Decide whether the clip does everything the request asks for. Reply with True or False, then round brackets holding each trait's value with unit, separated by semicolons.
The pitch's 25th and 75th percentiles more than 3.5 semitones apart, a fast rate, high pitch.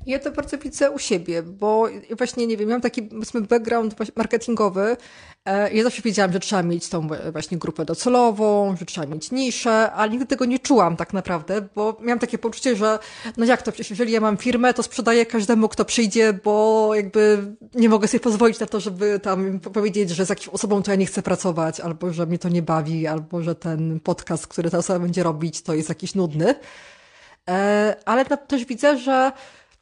True (4.4 semitones; 195 wpm; 215 Hz)